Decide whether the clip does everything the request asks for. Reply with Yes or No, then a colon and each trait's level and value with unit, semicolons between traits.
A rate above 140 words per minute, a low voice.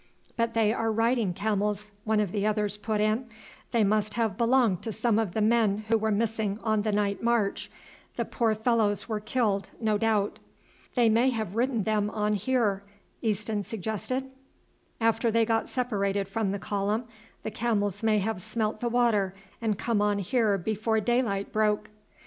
No: average, 170 wpm; high, 215 Hz